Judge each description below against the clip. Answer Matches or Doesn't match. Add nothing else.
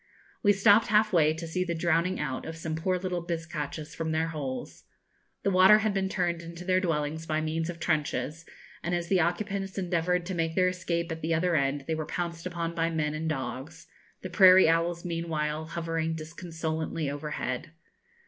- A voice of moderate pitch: Matches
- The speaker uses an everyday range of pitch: Doesn't match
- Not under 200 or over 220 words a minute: Doesn't match